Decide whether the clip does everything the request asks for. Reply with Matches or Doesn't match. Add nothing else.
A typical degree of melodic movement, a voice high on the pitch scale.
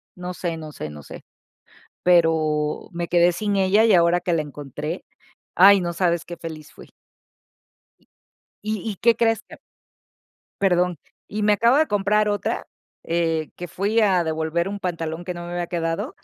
Doesn't match